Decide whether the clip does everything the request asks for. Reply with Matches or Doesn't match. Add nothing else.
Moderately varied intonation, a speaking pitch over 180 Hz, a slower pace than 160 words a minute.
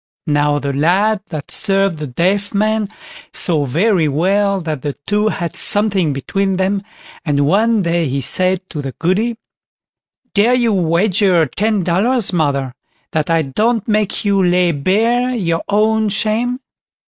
Matches